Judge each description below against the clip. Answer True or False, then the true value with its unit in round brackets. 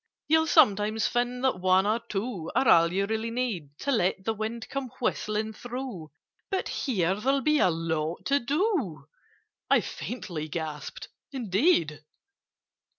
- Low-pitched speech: False (220 Hz)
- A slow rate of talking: False (145 wpm)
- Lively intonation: True (6.5 semitones)